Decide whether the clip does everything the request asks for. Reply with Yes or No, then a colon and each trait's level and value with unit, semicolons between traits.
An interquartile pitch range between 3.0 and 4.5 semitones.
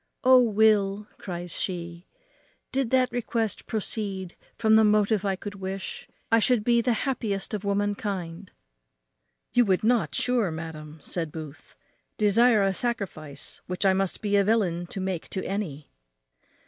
Yes: average, 3.4 semitones